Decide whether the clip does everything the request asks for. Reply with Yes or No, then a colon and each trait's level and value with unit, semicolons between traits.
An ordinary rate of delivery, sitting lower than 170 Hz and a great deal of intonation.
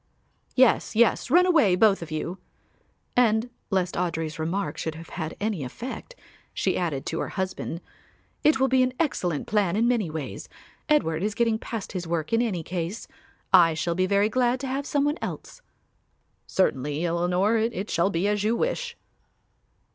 No: average, 170 wpm; high, 200 Hz; wide, 6.0 semitones